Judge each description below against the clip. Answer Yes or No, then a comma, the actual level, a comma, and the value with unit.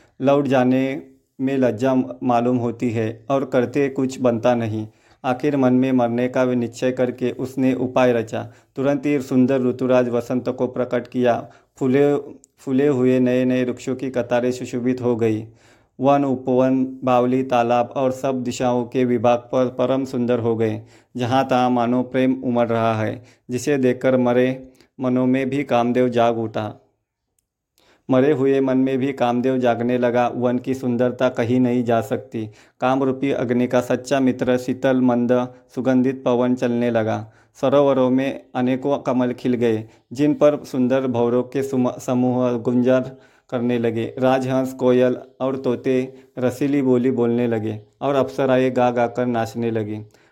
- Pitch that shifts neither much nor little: No, narrow, 1.4 semitones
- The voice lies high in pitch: No, low, 125 Hz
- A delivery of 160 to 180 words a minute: No, average, 150 wpm